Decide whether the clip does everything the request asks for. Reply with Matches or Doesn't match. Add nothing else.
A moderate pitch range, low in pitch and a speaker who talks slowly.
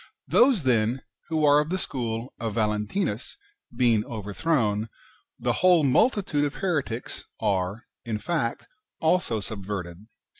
Doesn't match